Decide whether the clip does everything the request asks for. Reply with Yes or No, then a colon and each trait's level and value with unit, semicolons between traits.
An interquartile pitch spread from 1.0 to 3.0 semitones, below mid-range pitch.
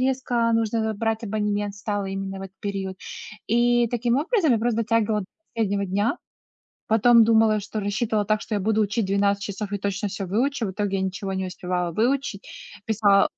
No: narrow, 2.5 semitones; high, 210 Hz